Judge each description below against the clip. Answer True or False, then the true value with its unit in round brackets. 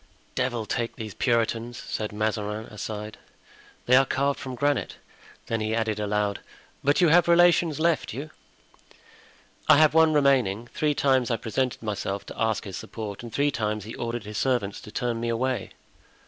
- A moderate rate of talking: True (170 wpm)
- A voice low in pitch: True (115 Hz)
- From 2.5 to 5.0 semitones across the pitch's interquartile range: True (4.5 semitones)